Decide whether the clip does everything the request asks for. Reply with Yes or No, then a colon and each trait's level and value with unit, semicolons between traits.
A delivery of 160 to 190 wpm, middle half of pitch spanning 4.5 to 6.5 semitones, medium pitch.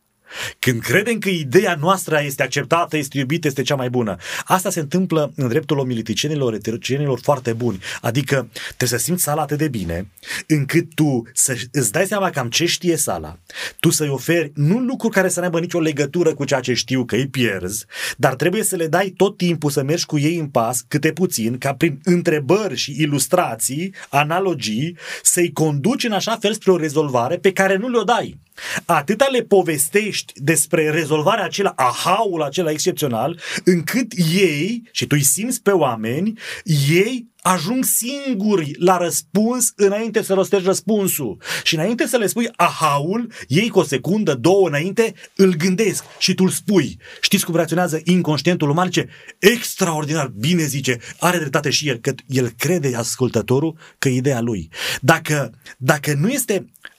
Yes: fast, 170 wpm; average, 5.1 semitones; medium, 165 Hz